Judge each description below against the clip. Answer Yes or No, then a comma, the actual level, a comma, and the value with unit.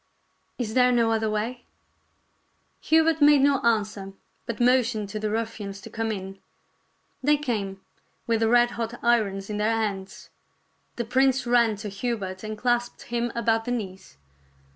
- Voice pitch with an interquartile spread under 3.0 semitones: Yes, narrow, 2.5 semitones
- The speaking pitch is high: Yes, high, 225 Hz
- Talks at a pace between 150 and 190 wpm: Yes, average, 160 wpm